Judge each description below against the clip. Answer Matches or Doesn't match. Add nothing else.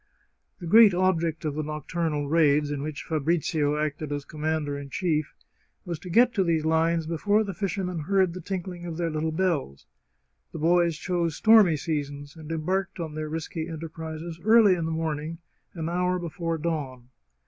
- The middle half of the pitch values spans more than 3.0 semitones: Doesn't match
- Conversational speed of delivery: Matches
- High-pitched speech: Doesn't match